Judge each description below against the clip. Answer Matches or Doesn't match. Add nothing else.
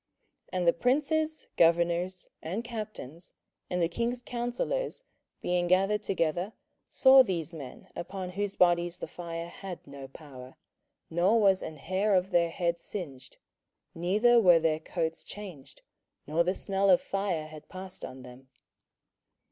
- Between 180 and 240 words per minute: Doesn't match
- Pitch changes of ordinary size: Matches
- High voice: Doesn't match